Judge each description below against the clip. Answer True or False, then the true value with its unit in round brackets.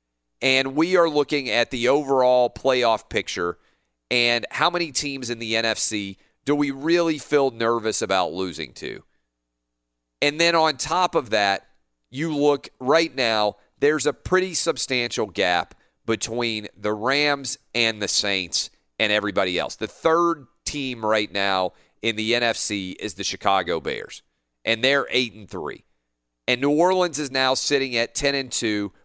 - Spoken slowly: False (155 wpm)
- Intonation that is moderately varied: False (6.3 semitones)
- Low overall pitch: True (120 Hz)